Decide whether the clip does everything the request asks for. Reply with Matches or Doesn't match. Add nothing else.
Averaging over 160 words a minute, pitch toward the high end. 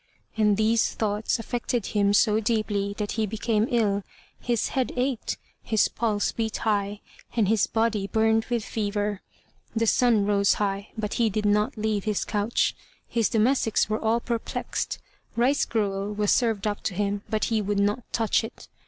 Matches